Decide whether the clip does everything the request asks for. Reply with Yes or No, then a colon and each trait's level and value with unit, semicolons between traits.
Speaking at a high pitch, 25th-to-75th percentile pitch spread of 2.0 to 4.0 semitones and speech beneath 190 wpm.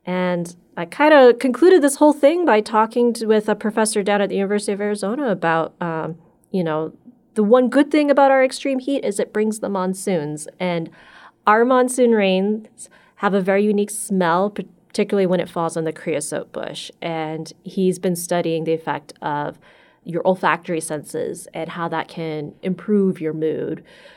No: high, 195 Hz; average, 4.6 semitones; average, 175 wpm